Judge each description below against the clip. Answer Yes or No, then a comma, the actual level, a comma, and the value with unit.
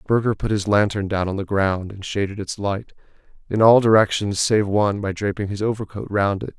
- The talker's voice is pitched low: Yes, low, 100 Hz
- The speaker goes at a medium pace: No, fast, 210 wpm